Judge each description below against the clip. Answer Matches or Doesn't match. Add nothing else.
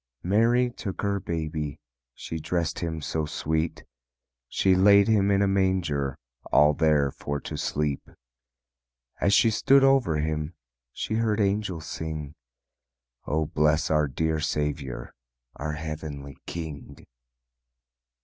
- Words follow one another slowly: Matches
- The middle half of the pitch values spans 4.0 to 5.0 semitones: Matches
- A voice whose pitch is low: Matches